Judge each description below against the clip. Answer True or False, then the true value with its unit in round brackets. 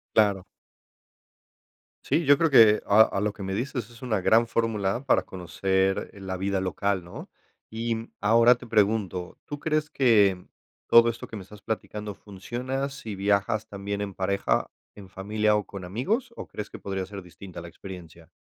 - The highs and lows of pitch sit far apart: False (3.2 semitones)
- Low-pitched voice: True (105 Hz)